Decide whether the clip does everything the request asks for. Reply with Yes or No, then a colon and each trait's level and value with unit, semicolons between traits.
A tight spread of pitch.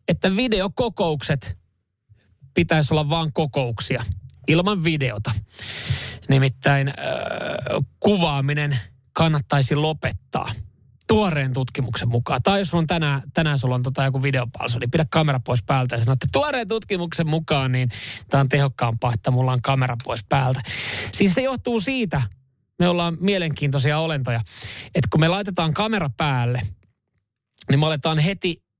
No: average, 5.1 semitones